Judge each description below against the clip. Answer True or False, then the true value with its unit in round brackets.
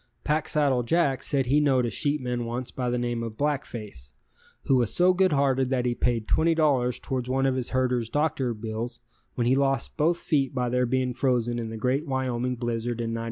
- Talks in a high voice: False (125 Hz)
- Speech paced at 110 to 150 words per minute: False (205 wpm)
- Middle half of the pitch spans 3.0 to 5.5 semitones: False (2.6 semitones)